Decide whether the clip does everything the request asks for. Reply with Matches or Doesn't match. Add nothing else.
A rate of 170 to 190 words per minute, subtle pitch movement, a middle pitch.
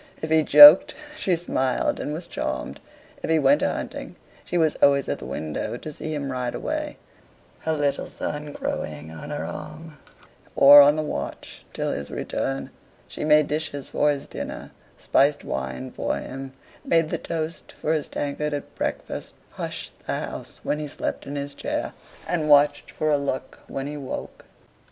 Matches